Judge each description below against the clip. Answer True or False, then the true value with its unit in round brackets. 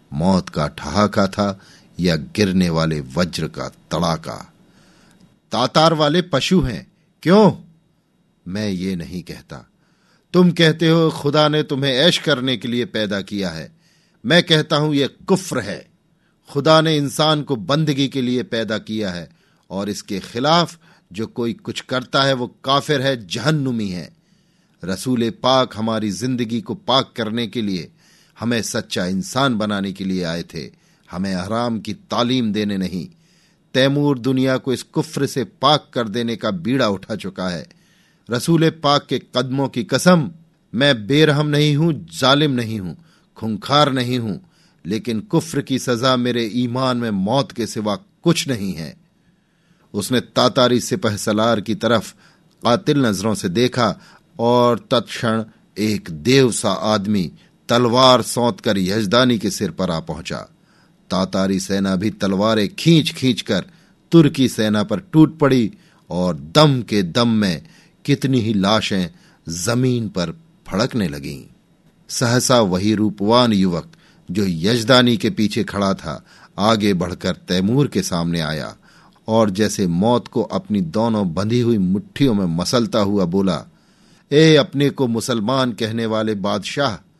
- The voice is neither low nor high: False (120 Hz)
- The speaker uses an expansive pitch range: True (6.2 semitones)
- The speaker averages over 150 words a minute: False (145 wpm)